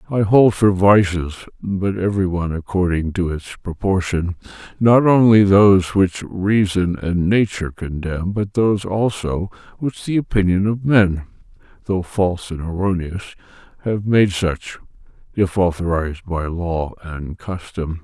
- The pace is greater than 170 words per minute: No, slow, 135 wpm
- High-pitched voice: No, very low, 95 Hz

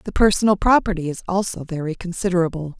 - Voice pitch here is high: No, medium, 180 Hz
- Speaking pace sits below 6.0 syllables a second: No, 6.5 syllables/s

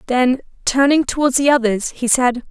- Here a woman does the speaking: Yes, female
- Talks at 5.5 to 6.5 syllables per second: No, 4.9 syllables/s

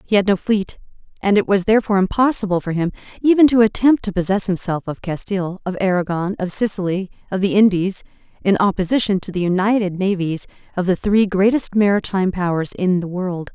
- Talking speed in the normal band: Yes, average, 180 wpm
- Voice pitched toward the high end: Yes, high, 195 Hz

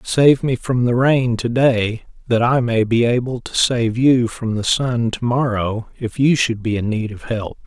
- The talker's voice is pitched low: Yes, low, 120 Hz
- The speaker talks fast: Yes, fast, 220 wpm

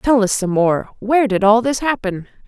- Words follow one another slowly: No, fast, 220 wpm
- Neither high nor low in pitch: No, high, 220 Hz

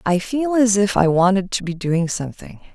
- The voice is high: Yes, high, 195 Hz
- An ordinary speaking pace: No, fast, 220 wpm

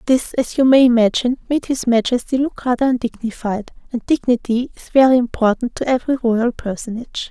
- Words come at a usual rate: Yes, average, 165 wpm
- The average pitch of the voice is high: Yes, high, 245 Hz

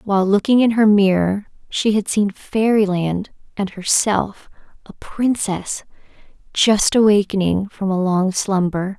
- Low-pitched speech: No, high, 200 Hz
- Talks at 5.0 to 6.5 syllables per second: No, 4.0 syllables/s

